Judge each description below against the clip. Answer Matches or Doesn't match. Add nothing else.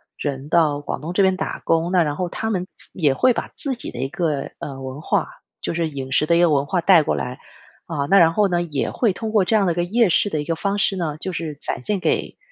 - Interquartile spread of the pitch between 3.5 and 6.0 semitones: Matches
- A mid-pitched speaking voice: Matches